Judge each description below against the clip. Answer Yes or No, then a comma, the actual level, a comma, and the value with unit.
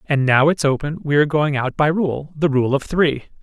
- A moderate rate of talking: No, fast, 230 wpm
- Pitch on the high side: No, medium, 145 Hz